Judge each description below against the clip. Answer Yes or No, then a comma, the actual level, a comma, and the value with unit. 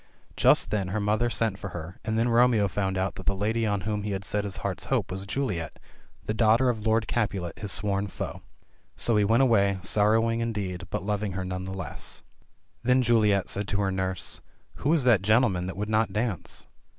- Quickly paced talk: Yes, fast, 210 wpm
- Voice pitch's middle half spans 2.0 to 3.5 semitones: Yes, average, 2.9 semitones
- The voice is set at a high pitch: No, low, 105 Hz